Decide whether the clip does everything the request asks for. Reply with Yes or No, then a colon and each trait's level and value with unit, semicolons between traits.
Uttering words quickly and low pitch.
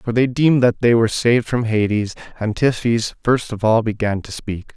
Yes: fast, 215 wpm; low, 115 Hz